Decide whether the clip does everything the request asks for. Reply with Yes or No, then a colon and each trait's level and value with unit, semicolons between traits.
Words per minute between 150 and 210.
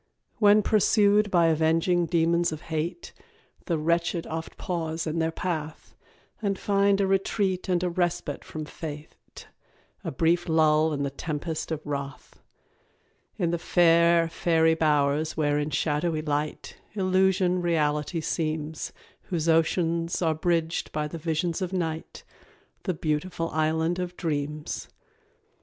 No: slow, 135 wpm